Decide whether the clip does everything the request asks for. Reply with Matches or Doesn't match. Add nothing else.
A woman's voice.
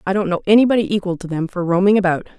Matches